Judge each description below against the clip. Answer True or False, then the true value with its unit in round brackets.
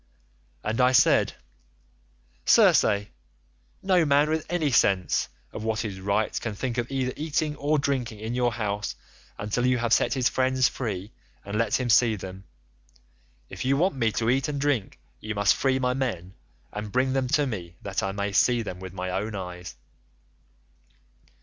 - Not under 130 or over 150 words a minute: False (175 wpm)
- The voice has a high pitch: False (115 Hz)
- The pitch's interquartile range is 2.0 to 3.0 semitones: False (4.6 semitones)